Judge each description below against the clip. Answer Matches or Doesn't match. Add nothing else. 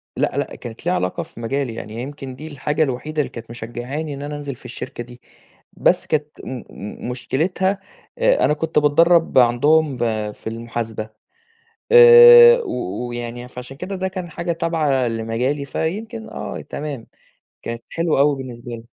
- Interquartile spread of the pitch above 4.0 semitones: Matches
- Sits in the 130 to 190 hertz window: Matches